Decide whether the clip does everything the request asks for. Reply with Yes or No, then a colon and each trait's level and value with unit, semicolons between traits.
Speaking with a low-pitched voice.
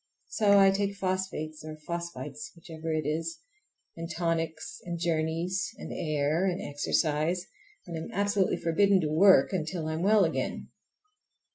No: medium, 165 Hz